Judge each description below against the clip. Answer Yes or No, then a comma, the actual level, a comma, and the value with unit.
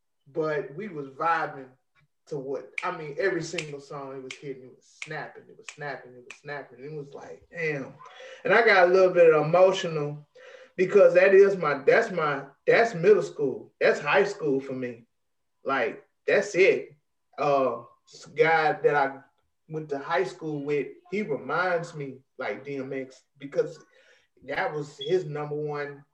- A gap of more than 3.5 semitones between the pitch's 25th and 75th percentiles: Yes, wide, 5.6 semitones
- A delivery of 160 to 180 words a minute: Yes, average, 165 wpm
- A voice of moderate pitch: Yes, medium, 155 Hz